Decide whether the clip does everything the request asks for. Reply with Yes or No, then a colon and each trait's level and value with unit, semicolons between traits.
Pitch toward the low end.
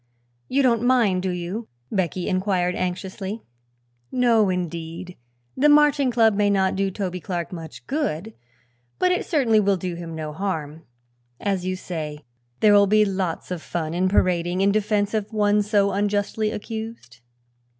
No: high, 195 Hz